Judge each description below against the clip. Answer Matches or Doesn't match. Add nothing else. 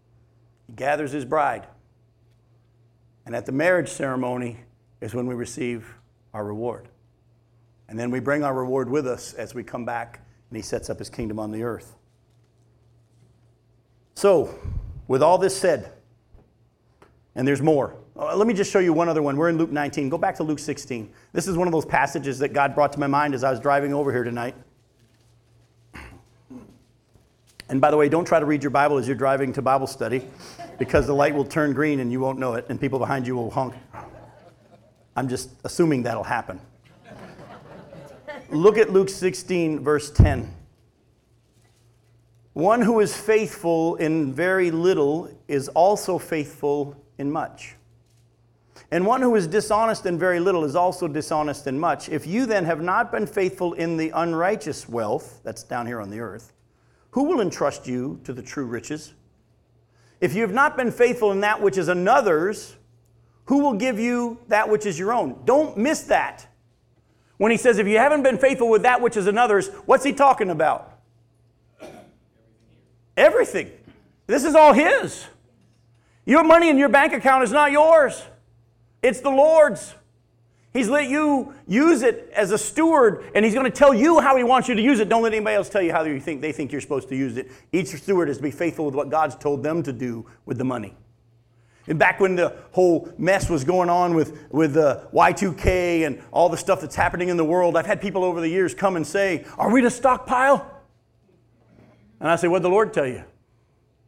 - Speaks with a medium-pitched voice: Matches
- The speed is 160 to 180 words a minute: Doesn't match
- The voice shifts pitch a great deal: Matches